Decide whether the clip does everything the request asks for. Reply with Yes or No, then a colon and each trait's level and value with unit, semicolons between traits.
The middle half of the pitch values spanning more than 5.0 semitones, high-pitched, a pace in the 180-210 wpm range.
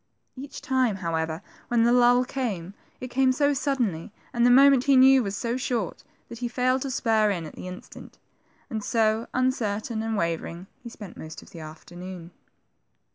Yes: wide, 5.5 semitones; high, 230 Hz; average, 185 wpm